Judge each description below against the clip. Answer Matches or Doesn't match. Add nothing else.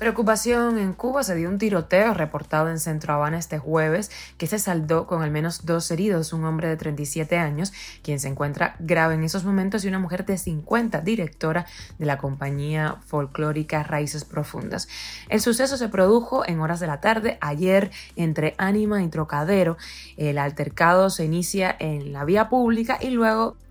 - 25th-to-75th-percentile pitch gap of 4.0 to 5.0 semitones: Matches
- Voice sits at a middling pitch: Matches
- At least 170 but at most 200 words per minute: Matches